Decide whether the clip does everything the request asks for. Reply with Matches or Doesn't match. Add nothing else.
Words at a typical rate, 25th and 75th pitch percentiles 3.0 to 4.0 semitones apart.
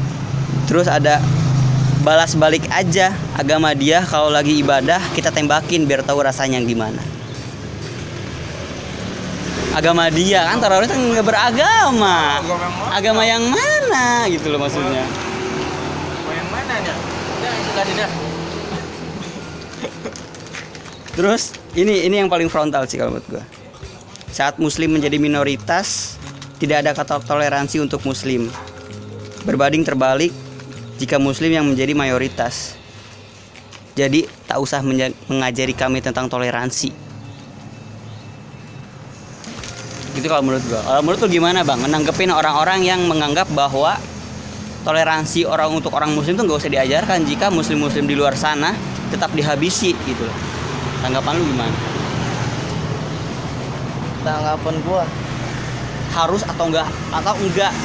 Matches